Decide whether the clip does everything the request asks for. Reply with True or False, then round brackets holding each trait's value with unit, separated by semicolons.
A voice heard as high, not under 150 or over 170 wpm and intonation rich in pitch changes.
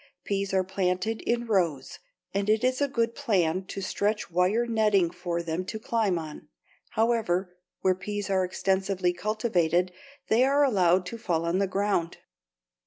False (195 Hz; 160 wpm; 3.5 semitones)